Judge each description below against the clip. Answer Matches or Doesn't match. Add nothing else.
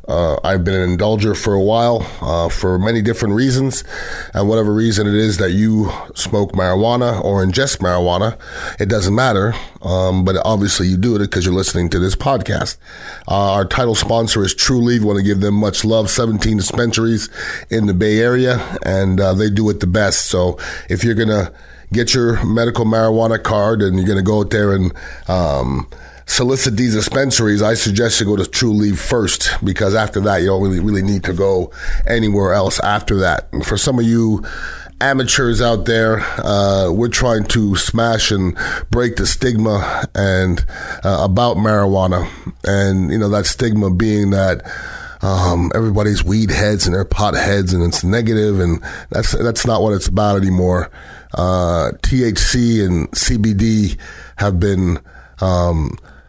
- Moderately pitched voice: Doesn't match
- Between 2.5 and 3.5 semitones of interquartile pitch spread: Matches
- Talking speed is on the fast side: Doesn't match